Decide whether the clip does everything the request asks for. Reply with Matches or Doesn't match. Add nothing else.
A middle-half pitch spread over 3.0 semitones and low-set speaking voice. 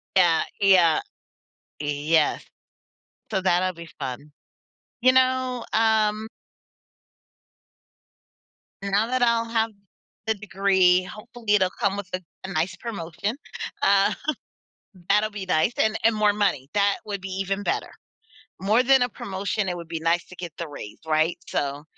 Doesn't match